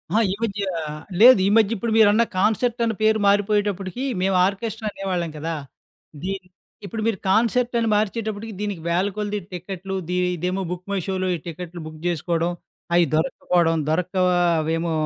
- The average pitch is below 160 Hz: No, high, 195 Hz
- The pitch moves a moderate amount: Yes, average, 3.5 semitones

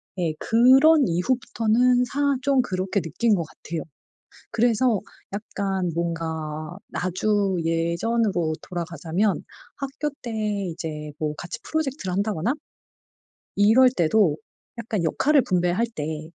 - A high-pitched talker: Yes, high, 195 Hz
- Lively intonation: Yes, wide, 6.2 semitones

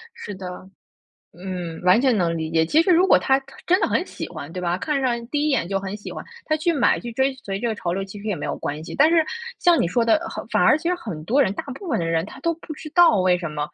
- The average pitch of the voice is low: No, high, 225 Hz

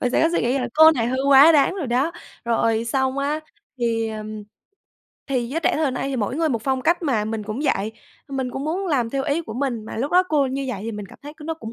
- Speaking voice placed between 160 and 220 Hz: No, very high, 265 Hz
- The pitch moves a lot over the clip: No, average, 4.5 semitones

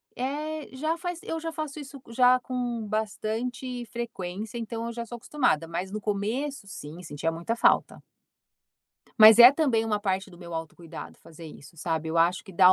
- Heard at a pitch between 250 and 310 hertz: No, high, 225 Hz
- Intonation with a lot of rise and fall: Yes, wide, 5.9 semitones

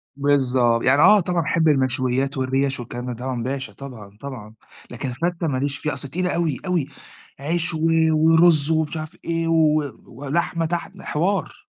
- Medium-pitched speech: Yes, medium, 145 Hz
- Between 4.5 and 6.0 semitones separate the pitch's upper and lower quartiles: No, average, 4.1 semitones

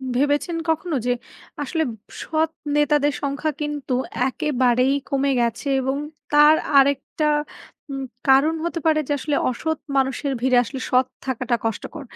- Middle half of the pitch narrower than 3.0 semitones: Yes, narrow, 2.6 semitones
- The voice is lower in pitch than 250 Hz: No, very high, 280 Hz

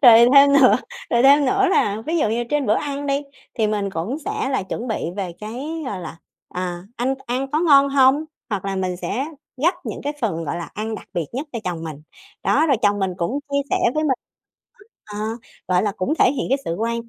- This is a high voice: Yes, high, 235 Hz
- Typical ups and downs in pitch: No, wide, 6.4 semitones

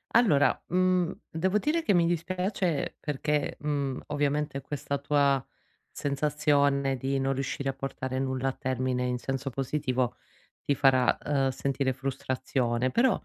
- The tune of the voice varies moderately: No, narrow, 2.2 semitones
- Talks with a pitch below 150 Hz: Yes, medium, 140 Hz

